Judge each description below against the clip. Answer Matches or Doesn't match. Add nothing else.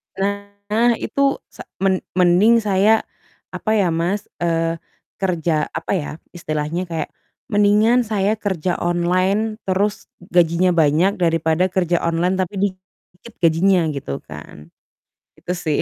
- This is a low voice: Doesn't match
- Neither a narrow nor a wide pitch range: Matches